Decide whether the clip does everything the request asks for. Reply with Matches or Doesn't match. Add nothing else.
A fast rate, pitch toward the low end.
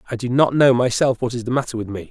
Matches